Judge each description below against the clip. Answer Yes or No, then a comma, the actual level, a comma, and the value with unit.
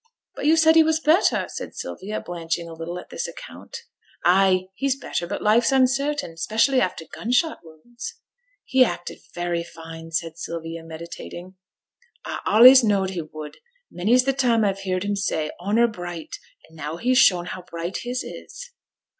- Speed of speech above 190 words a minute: No, average, 170 wpm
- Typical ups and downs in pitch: No, wide, 7.0 semitones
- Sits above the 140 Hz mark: Yes, high, 190 Hz